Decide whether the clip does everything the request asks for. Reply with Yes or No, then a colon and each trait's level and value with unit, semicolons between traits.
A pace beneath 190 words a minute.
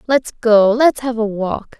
No: average, 200 wpm